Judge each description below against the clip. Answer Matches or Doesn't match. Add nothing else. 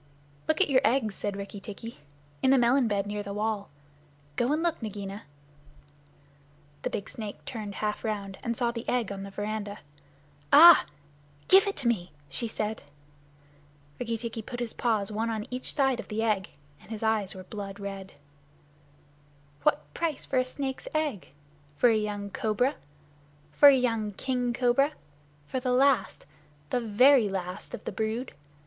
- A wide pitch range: Doesn't match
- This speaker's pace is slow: Doesn't match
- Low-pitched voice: Doesn't match